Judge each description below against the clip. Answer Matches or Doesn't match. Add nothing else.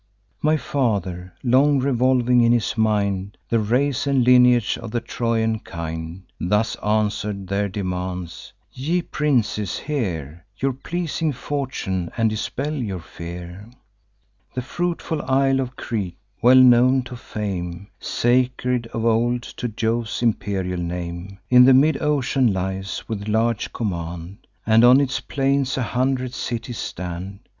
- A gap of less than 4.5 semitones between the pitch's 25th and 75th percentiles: Doesn't match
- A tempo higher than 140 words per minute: Doesn't match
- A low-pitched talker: Matches